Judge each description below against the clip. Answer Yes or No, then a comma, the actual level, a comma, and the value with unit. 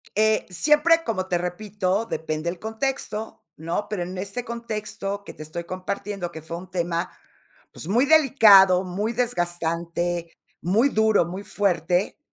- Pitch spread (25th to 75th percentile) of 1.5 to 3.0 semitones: No, average, 3.9 semitones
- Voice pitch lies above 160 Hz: Yes, high, 190 Hz